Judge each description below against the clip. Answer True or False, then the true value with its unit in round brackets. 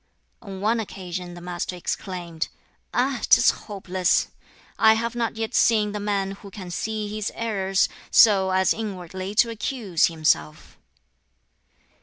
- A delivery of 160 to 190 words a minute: False (135 wpm)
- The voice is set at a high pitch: True (195 Hz)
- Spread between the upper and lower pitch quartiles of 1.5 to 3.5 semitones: True (3.2 semitones)